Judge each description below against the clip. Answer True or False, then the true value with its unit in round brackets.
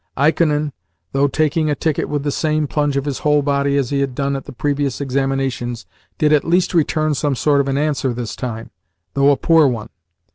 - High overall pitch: False (140 Hz)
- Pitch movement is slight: True (1.8 semitones)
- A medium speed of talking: False (210 wpm)